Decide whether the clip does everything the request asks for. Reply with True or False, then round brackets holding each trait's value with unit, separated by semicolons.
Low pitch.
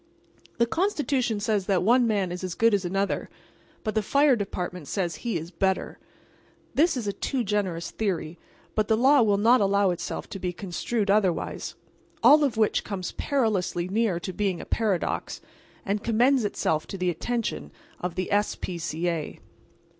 False (205 Hz)